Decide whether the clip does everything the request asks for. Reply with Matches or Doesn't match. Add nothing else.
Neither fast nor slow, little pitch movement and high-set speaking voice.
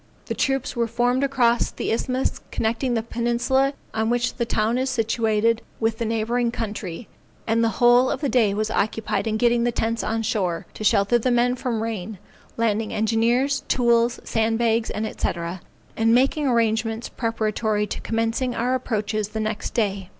Matches